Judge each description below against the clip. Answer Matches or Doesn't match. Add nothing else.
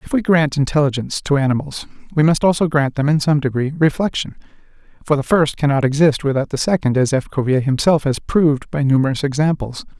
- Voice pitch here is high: Doesn't match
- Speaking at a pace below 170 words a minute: Doesn't match